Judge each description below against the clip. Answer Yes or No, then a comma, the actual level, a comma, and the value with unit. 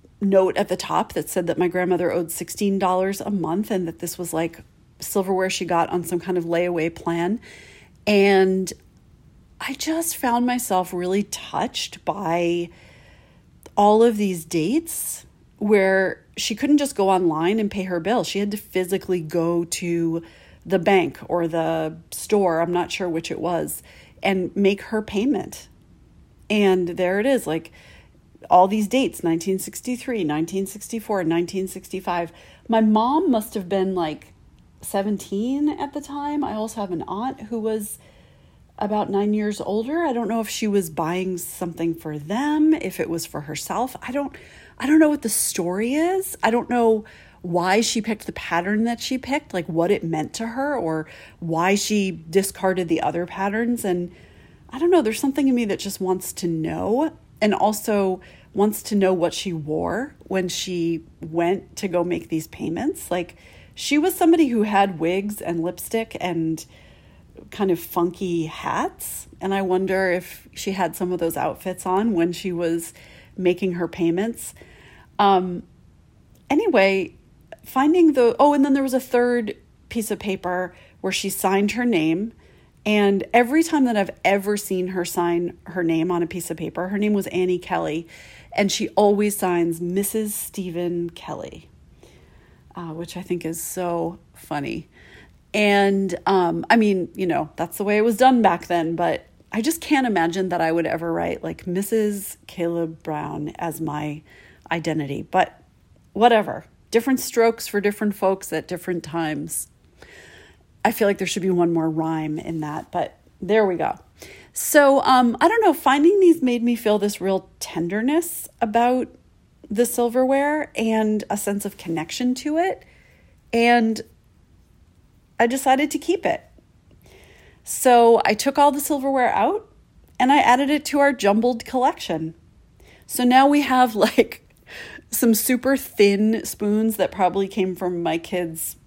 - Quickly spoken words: No, average, 165 wpm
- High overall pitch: Yes, high, 195 Hz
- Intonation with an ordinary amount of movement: Yes, average, 4.9 semitones